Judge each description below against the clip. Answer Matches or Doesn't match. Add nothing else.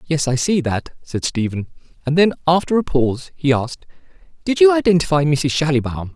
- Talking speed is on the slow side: Doesn't match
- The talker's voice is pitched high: Doesn't match